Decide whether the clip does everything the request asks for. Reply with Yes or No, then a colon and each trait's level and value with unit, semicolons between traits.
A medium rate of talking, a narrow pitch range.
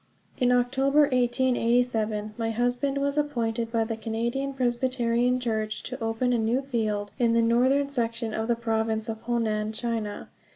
Yes: average, 155 wpm; narrow, 2.0 semitones